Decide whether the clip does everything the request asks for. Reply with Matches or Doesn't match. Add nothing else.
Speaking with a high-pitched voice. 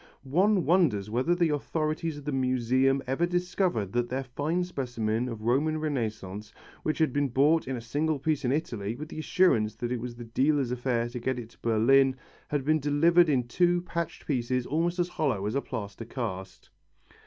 Doesn't match